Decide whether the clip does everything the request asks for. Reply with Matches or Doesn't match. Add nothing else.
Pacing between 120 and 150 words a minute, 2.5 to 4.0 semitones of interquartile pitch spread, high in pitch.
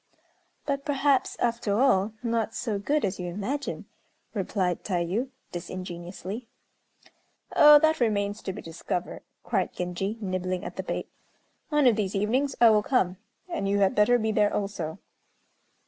Doesn't match